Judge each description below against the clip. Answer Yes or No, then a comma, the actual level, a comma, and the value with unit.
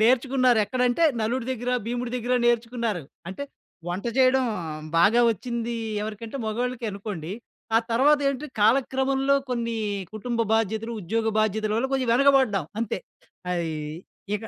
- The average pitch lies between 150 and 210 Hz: No, high, 235 Hz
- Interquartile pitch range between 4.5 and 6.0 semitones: No, average, 2.8 semitones